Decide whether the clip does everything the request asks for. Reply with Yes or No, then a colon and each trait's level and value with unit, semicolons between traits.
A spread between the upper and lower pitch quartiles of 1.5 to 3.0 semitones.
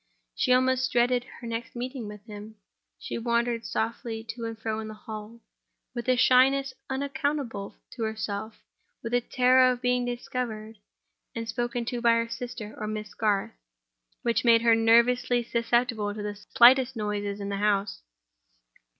Yes: narrow, 2.4 semitones